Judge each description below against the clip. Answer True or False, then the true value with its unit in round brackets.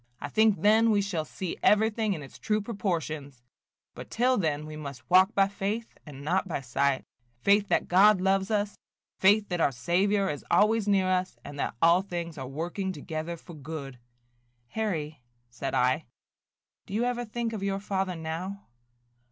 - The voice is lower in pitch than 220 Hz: True (185 Hz)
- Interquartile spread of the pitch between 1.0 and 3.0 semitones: False (4.9 semitones)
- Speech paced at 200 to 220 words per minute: False (175 wpm)